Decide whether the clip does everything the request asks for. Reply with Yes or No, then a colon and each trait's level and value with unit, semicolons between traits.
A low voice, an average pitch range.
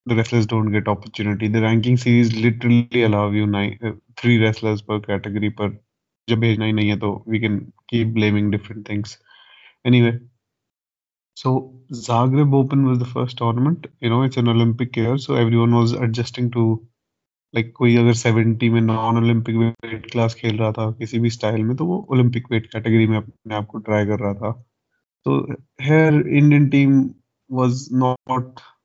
No: low, 115 Hz; narrow, 2.2 semitones